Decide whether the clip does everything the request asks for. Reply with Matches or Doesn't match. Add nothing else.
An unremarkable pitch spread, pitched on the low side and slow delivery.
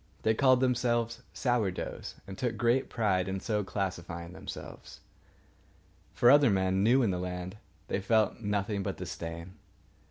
Doesn't match